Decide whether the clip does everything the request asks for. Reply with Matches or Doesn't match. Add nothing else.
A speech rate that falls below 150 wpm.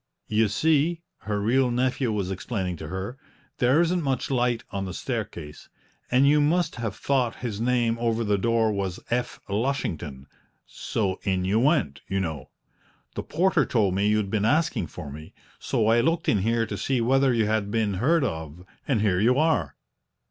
Doesn't match